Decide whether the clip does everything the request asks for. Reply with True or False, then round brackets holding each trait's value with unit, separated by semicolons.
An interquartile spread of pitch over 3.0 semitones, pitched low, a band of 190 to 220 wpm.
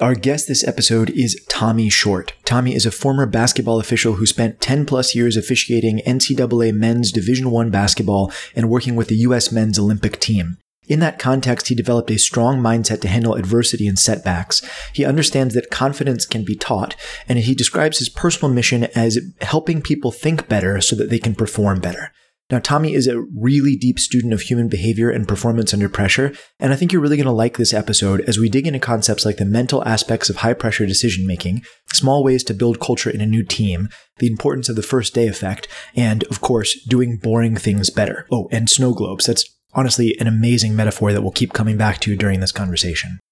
False (2.7 semitones; 115 Hz; 205 wpm)